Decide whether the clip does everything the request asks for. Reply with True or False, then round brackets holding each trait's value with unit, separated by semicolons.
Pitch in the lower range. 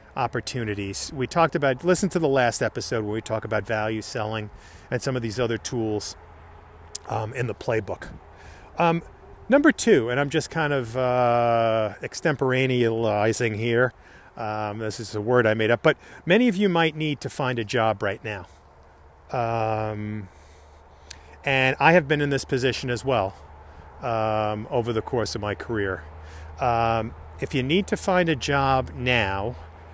True (115 Hz)